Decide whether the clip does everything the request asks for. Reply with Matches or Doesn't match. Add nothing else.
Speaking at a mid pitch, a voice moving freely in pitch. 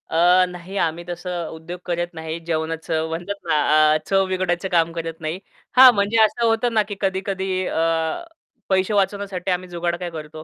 Doesn't match